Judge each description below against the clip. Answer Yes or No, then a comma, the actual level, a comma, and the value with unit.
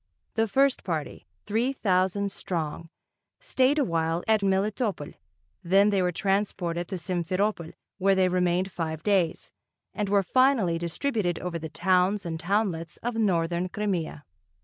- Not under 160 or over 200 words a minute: No, average, 140 wpm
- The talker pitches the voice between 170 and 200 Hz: Yes, medium, 185 Hz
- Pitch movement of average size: Yes, average, 3.5 semitones